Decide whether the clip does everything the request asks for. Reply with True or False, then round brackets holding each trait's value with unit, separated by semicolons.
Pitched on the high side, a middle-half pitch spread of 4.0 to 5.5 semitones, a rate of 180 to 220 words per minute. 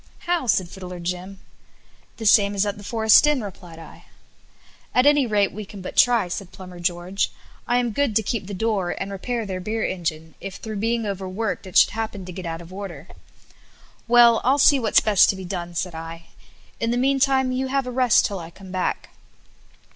True (200 Hz; 4.4 semitones; 205 wpm)